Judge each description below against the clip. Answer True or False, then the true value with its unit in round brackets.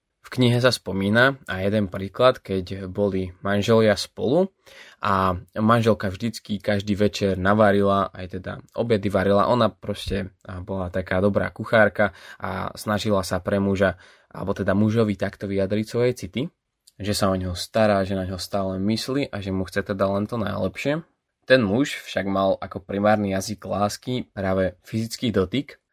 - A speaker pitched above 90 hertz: True (100 Hz)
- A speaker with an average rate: True (155 wpm)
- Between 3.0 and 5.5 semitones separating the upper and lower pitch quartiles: False (2.4 semitones)